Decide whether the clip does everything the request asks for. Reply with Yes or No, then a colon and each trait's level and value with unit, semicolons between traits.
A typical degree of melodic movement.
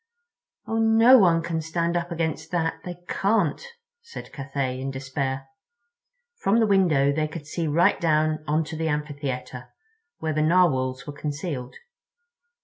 Yes: average, 3.5 semitones